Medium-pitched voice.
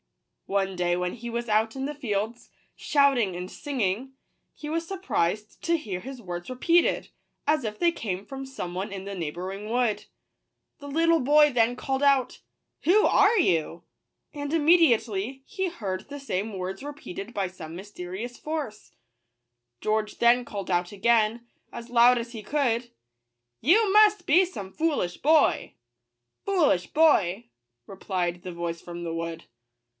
No: high, 230 Hz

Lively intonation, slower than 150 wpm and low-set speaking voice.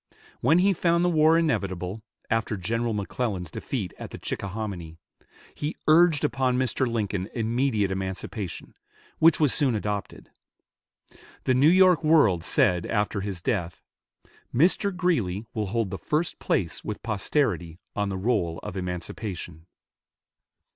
Yes: wide, 7.4 semitones; slow, 135 wpm; low, 110 Hz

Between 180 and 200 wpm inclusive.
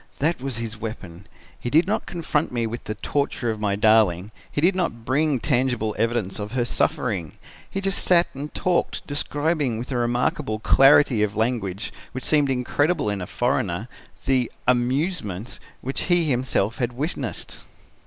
No: average, 165 wpm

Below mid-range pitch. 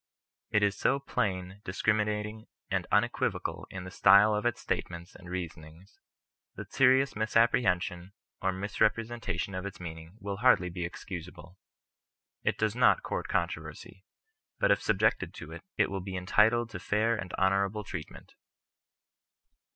Yes: very low, 95 Hz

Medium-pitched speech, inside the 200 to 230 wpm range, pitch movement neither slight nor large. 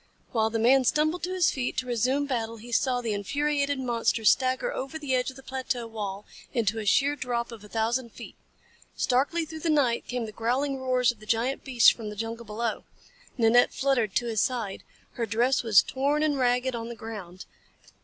No: high, 245 Hz; fast, 205 wpm; average, 3.0 semitones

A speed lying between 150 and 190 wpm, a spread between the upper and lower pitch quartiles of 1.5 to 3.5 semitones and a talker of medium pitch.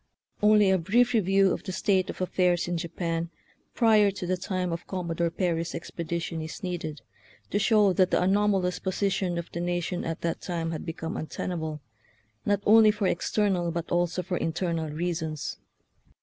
Yes: average, 175 wpm; narrow, 2.6 semitones; medium, 180 Hz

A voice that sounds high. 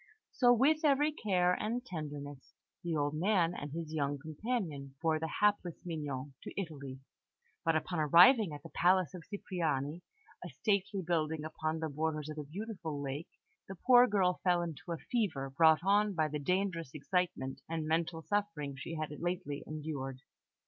No: medium, 165 Hz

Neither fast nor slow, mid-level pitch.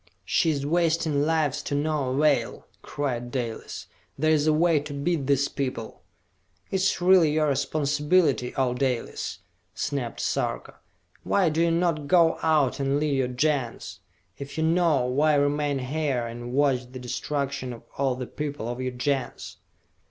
Yes: average, 160 wpm; medium, 145 Hz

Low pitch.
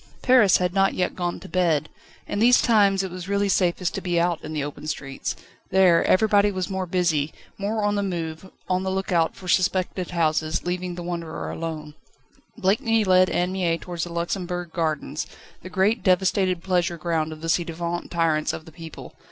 No: medium, 180 Hz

